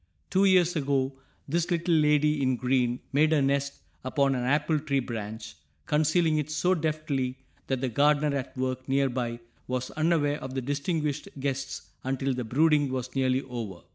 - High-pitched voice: No, medium, 140 Hz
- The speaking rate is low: No, average, 170 wpm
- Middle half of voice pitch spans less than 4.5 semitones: Yes, average, 3.0 semitones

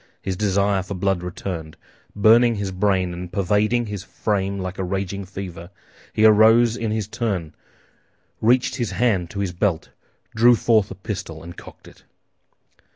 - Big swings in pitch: No, average, 3.0 semitones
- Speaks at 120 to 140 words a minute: No, average, 155 wpm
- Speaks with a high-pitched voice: No, low, 100 Hz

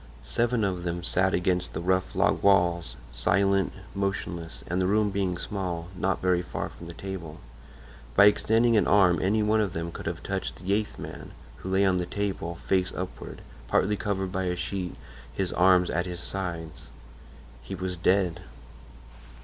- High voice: No, very low, 95 Hz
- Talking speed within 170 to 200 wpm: Yes, average, 175 wpm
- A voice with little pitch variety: Yes, narrow, 2.0 semitones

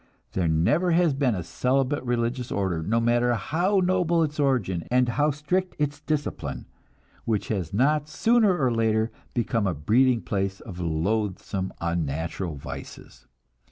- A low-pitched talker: Yes, low, 120 Hz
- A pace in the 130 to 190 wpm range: Yes, average, 145 wpm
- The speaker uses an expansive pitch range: Yes, wide, 7.4 semitones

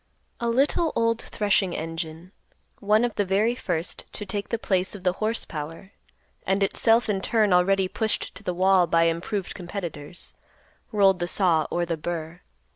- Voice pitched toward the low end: No, high, 190 Hz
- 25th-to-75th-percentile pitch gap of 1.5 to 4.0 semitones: Yes, average, 3.5 semitones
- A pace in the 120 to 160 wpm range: No, average, 170 wpm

